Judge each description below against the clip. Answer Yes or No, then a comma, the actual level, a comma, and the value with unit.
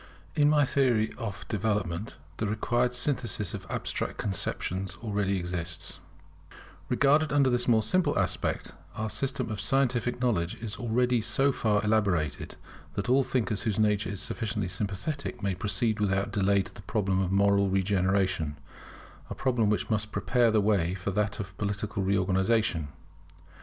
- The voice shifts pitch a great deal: No, average, 3.8 semitones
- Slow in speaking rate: No, average, 150 wpm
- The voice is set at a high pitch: No, low, 105 Hz